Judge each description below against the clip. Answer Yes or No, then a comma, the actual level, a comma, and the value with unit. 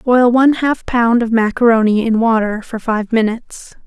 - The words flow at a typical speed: Yes, average, 170 wpm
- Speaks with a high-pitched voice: Yes, high, 230 Hz